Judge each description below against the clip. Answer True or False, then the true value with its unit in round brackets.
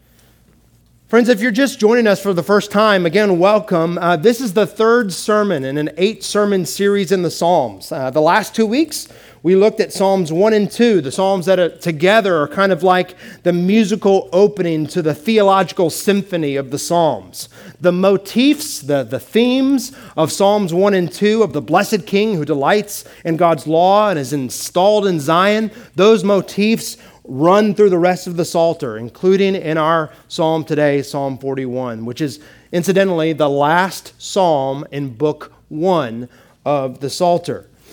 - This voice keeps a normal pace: True (170 wpm)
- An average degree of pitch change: True (4.6 semitones)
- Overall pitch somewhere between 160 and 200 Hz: True (185 Hz)